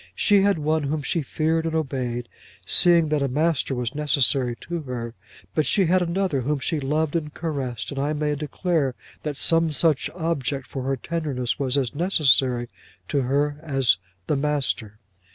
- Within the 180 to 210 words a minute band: No, average, 170 wpm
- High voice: No, medium, 145 Hz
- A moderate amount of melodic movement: Yes, average, 3.4 semitones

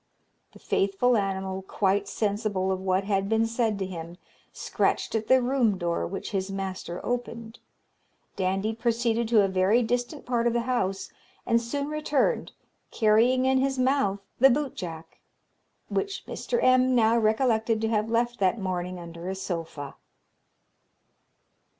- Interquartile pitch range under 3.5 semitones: No, average, 4.1 semitones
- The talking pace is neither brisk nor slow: Yes, average, 145 wpm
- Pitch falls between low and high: No, high, 220 Hz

